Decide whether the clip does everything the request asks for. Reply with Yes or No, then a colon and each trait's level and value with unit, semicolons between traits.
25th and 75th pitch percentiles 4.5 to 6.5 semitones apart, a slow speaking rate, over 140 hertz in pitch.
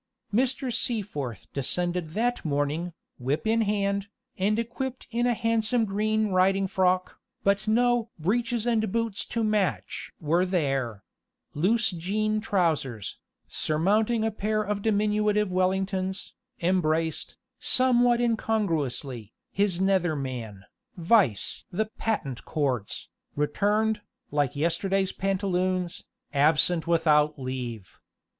Yes: wide, 5.6 semitones; slow, 110 wpm; high, 190 Hz